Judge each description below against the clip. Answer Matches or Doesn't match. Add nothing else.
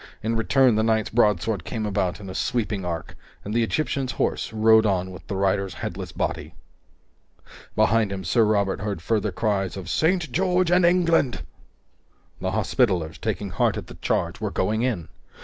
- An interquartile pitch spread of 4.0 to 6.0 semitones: Doesn't match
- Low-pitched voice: Matches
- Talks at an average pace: Matches